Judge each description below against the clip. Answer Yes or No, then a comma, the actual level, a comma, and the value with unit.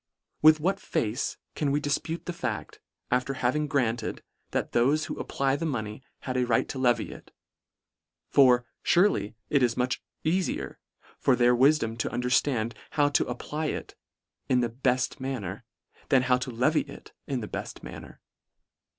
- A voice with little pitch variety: No, average, 3.1 semitones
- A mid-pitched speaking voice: No, low, 130 Hz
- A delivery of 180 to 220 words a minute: No, average, 160 wpm